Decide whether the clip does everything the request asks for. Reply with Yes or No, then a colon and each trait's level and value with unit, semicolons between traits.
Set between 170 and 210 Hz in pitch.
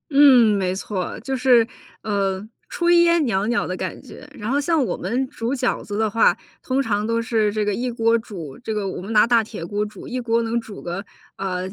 No: high, 225 Hz